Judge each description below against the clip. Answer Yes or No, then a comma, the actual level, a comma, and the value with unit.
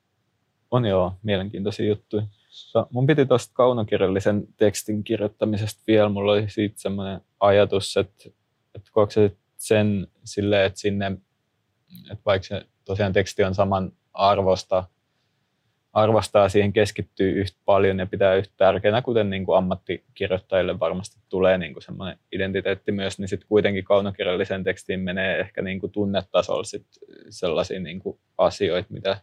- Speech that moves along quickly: No, average, 135 wpm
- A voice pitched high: No, low, 100 Hz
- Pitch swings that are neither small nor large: No, narrow, 1.7 semitones